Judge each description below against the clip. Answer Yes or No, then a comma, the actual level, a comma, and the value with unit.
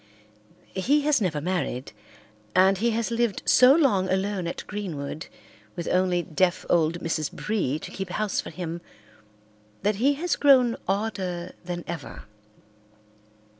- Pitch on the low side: No, high, 190 Hz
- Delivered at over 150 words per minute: No, slow, 135 wpm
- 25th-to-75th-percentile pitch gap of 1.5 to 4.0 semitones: No, average, 4.4 semitones